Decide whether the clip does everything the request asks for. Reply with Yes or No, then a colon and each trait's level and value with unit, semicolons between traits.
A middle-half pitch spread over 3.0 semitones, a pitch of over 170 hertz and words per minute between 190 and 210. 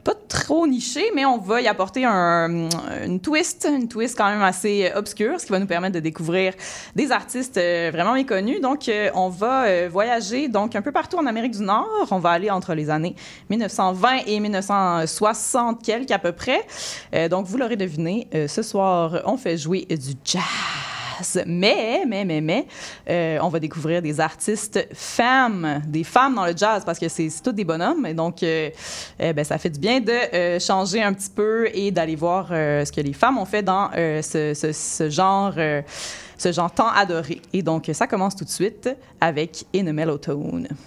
Yes: average, 5.3 semitones; high, 190 Hz; average, 195 wpm